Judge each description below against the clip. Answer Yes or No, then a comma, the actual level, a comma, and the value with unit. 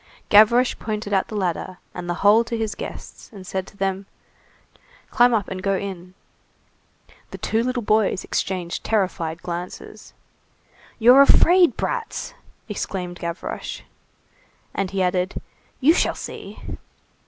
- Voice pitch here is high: Yes, high, 195 Hz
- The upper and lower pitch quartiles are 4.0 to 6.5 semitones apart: No, average, 3.5 semitones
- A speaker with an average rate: No, slow, 130 wpm